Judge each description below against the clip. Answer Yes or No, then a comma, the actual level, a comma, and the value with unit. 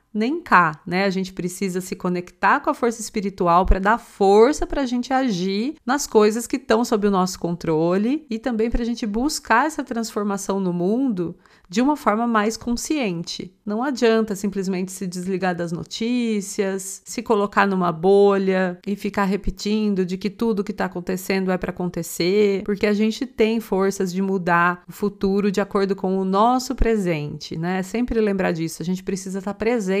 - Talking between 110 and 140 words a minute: No, average, 180 wpm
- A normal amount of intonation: Yes, average, 3.4 semitones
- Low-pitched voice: No, high, 205 Hz